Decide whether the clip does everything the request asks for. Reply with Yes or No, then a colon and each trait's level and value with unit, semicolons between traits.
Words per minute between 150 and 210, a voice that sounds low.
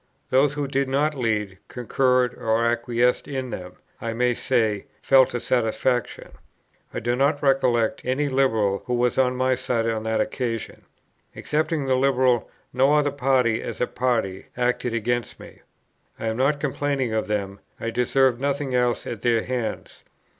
Yes: average, 160 wpm; low, 125 Hz